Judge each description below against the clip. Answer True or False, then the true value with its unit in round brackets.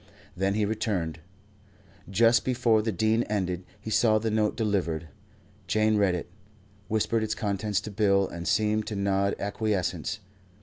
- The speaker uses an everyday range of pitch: False (2.1 semitones)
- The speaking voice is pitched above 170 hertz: False (105 Hz)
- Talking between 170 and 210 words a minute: False (145 wpm)